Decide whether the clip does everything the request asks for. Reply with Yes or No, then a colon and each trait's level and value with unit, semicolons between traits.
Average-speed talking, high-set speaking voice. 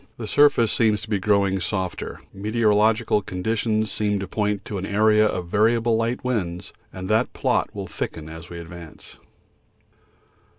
No: average, 160 wpm; low, 105 Hz